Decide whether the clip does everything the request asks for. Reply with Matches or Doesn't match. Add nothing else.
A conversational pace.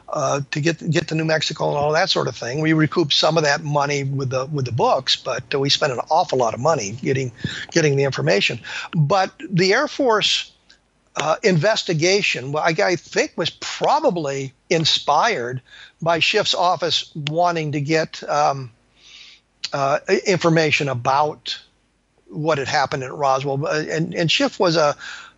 Matches